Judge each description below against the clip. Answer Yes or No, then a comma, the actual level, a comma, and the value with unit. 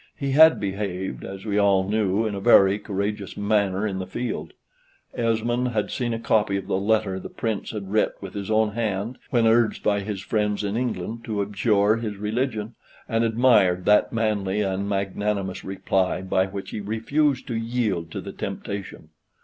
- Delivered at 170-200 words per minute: Yes, average, 180 wpm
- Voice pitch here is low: Yes, low, 105 Hz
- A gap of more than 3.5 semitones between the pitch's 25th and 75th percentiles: No, narrow, 2.6 semitones